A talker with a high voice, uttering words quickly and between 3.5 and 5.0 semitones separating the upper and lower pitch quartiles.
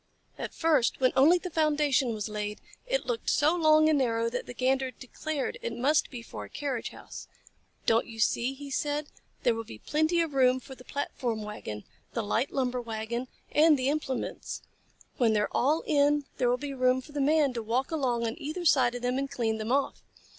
Yes: very high, 260 Hz; fast, 210 wpm; average, 4.0 semitones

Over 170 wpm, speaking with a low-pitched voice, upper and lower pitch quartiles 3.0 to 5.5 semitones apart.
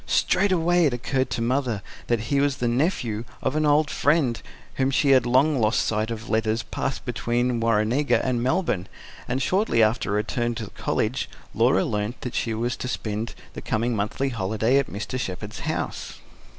Yes: average, 180 wpm; low, 120 Hz; average, 3.5 semitones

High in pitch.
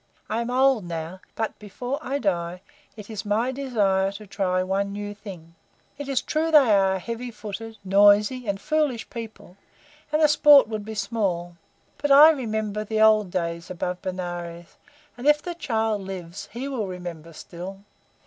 Yes: high, 210 Hz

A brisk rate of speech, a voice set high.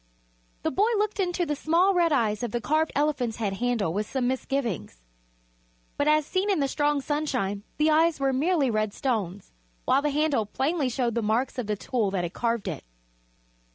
No: average, 190 wpm; very high, 265 Hz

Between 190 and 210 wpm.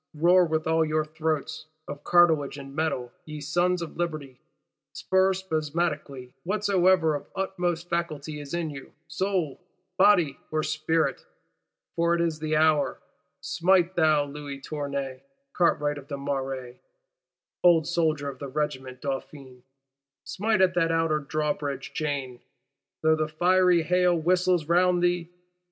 No: slow, 135 wpm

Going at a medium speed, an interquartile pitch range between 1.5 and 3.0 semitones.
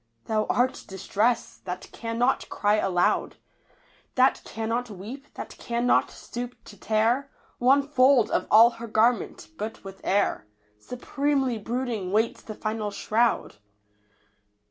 No: slow, 125 wpm; average, 2.7 semitones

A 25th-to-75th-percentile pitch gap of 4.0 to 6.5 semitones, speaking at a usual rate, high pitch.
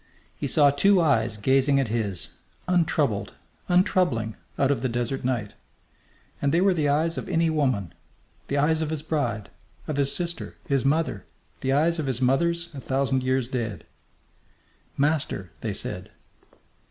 No: average, 4.3 semitones; average, 155 wpm; medium, 140 Hz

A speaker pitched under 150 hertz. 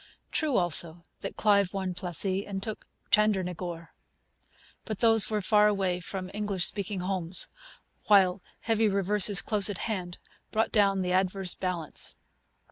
No: high, 195 Hz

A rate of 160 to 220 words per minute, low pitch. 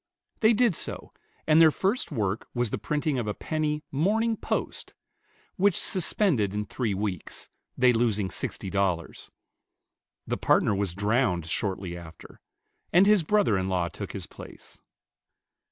No: average, 145 wpm; low, 115 Hz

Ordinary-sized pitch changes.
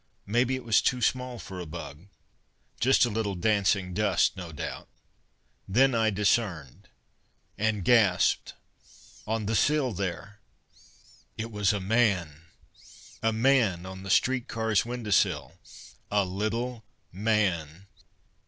Yes: average, 3.7 semitones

